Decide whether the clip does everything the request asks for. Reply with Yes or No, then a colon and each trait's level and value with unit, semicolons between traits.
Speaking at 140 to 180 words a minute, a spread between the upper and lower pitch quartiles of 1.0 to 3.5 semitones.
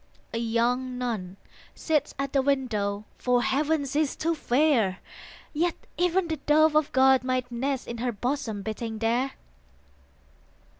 No: average, 145 wpm; average, 4.1 semitones